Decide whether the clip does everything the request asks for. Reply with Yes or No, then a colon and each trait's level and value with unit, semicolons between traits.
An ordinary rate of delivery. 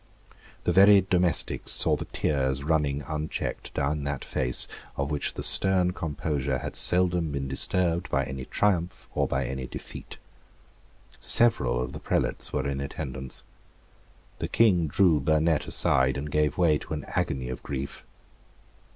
Yes: average, 150 wpm